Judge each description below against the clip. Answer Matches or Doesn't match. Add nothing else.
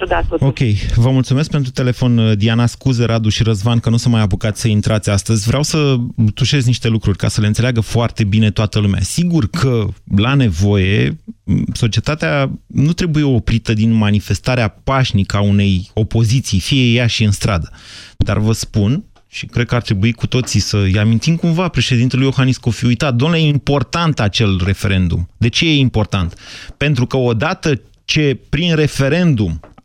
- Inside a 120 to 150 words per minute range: Doesn't match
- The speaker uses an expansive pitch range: Doesn't match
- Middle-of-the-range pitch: Doesn't match